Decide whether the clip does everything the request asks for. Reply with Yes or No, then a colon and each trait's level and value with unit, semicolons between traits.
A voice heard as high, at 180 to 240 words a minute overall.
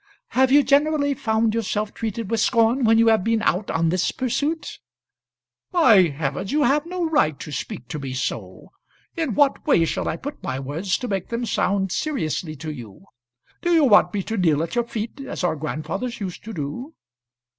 Yes: high, 220 Hz; average, 195 wpm